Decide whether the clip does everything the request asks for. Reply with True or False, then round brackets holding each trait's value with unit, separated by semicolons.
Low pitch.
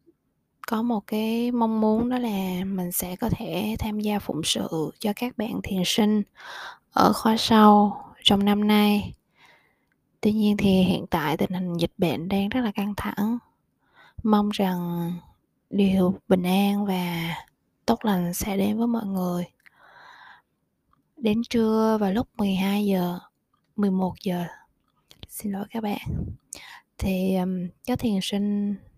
False (205 Hz)